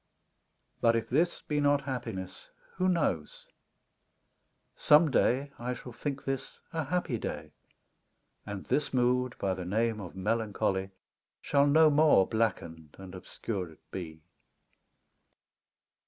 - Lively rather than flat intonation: Yes, wide, 6.9 semitones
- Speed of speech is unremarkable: No, slow, 120 wpm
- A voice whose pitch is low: Yes, low, 120 Hz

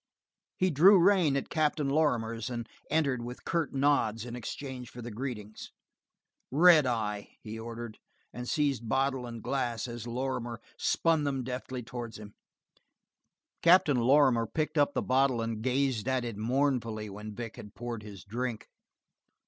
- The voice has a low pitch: Yes, low, 125 Hz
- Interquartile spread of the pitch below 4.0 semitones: Yes, average, 3.4 semitones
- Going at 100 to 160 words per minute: Yes, average, 150 wpm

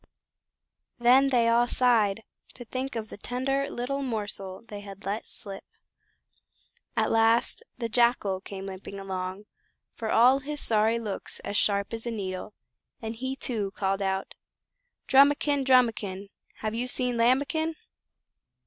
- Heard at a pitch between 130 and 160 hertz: No, high, 230 Hz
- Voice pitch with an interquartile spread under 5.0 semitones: Yes, average, 4.0 semitones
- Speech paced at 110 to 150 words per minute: Yes, average, 140 wpm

